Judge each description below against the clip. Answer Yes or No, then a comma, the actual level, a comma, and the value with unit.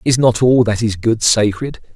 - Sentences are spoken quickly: Yes, fast, 215 wpm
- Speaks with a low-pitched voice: Yes, low, 115 Hz